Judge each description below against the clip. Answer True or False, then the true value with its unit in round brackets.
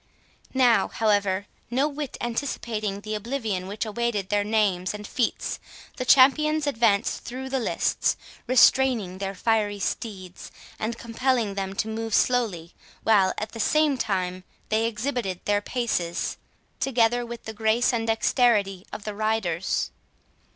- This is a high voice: True (220 Hz)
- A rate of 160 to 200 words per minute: False (135 wpm)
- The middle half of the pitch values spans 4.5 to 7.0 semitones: False (3.3 semitones)